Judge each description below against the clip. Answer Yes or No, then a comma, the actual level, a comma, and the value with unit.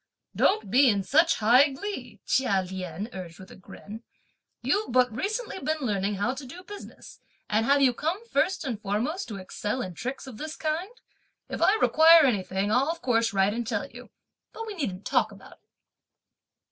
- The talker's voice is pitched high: Yes, very high, 250 Hz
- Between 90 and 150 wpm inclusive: No, average, 185 wpm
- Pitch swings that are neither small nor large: No, wide, 7.4 semitones